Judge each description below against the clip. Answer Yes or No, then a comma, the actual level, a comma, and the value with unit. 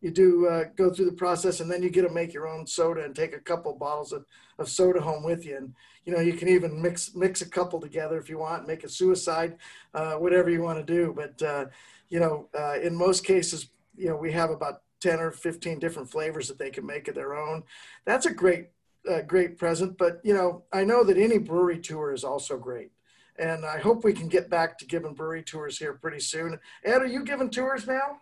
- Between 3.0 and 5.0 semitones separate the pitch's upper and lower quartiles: No, narrow, 2.5 semitones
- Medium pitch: Yes, medium, 170 Hz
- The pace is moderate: No, fast, 240 wpm